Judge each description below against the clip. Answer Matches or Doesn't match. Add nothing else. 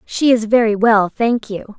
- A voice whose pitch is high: Matches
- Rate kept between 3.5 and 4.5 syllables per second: Matches